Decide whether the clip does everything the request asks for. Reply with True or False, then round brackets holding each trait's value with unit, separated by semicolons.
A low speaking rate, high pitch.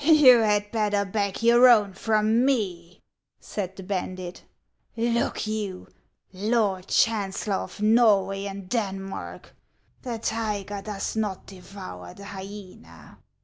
True (120 wpm; 205 Hz)